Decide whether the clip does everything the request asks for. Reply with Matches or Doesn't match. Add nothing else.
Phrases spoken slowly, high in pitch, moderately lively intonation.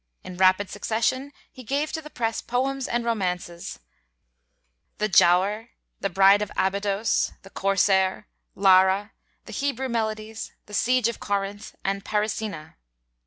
Matches